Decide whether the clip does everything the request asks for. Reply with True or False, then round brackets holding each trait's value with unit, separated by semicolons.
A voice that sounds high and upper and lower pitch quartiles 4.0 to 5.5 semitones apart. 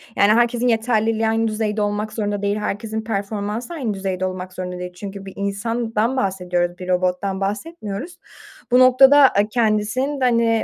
False (215 Hz; 2.9 semitones)